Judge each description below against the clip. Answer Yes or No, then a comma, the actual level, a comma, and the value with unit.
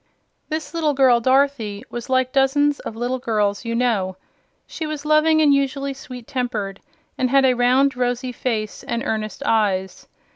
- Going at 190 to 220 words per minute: No, average, 160 wpm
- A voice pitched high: Yes, very high, 255 Hz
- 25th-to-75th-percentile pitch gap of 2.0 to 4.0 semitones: Yes, average, 3.6 semitones